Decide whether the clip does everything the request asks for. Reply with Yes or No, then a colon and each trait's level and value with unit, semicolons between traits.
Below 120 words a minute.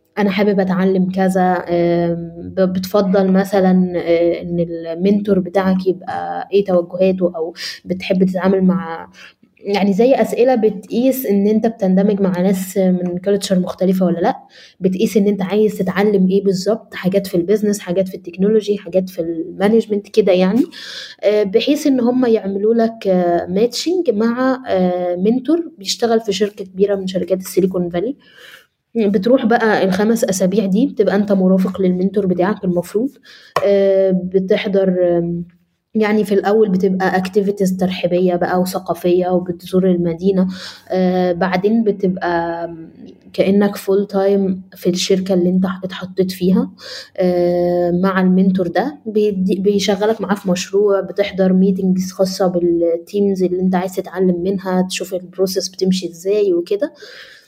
No: average, 125 wpm